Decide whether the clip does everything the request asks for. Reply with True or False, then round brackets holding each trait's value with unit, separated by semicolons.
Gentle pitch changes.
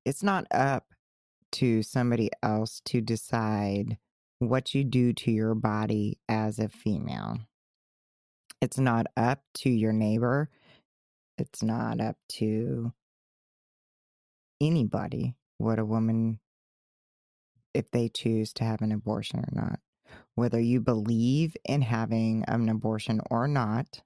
True (2.1 semitones)